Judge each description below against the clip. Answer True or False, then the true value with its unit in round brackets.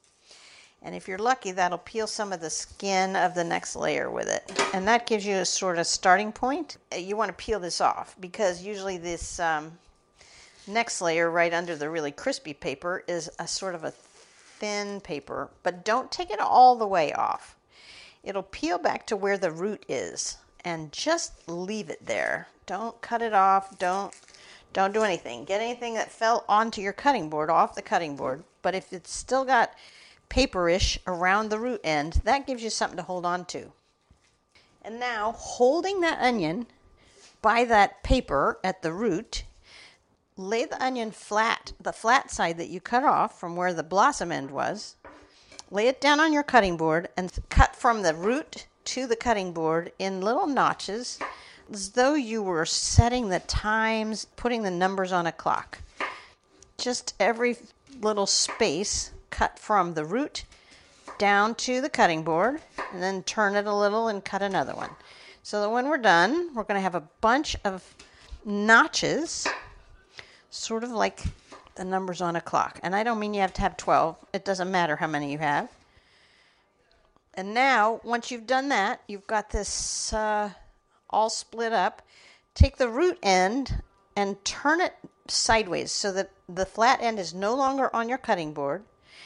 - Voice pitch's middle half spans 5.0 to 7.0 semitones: False (4.5 semitones)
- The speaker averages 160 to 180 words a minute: True (175 wpm)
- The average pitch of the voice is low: False (205 Hz)